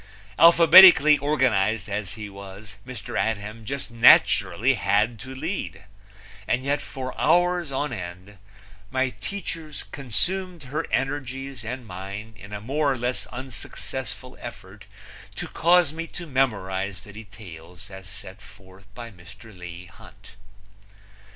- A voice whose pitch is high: No, low, 115 Hz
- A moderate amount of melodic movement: No, wide, 5.9 semitones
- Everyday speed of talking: No, slow, 130 wpm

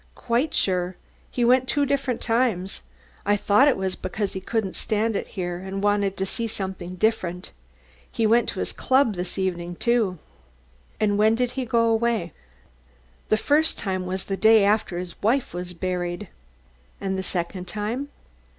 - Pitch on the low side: No, high, 205 Hz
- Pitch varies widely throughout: No, average, 4.0 semitones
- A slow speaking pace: No, average, 170 wpm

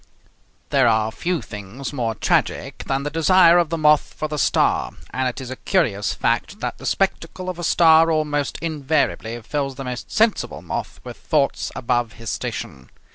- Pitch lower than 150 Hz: Yes, medium, 140 Hz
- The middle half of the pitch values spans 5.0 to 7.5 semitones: Yes, average, 5.3 semitones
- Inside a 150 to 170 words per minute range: No, average, 180 wpm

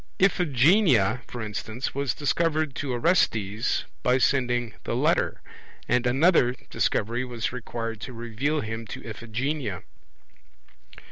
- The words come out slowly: Yes, slow, 115 wpm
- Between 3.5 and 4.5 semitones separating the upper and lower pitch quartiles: Yes, average, 3.8 semitones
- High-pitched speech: No, low, 125 Hz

